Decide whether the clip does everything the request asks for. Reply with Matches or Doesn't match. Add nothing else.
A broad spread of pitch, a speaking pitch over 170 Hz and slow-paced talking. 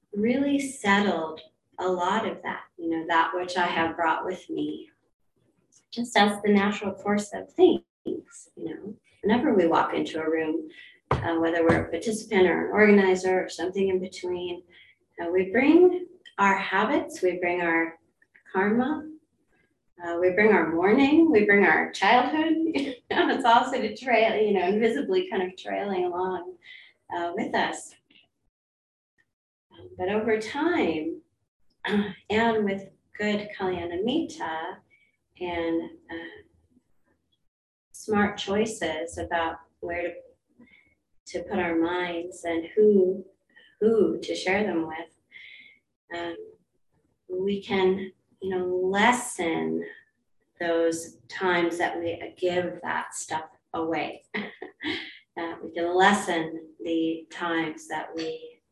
Matches